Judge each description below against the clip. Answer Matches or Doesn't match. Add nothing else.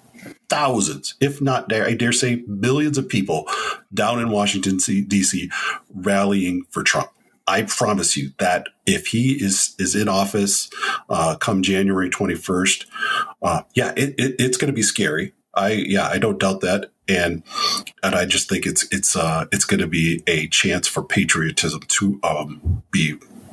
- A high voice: Doesn't match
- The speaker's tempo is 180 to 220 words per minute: Doesn't match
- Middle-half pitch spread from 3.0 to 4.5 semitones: Doesn't match